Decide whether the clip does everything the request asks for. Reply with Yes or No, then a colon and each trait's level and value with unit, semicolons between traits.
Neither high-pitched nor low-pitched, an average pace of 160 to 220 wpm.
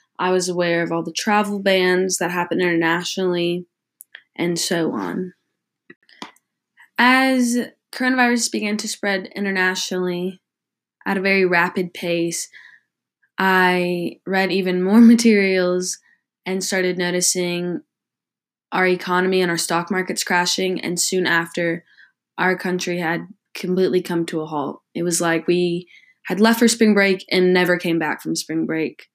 No: medium, 180 Hz; average, 140 wpm